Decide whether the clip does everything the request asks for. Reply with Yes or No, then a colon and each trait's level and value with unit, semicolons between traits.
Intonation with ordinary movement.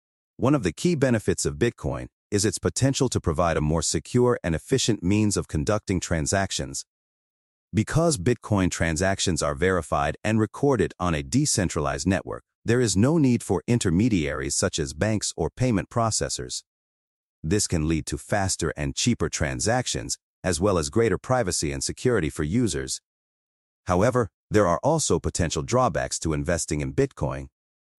No: wide, 6.7 semitones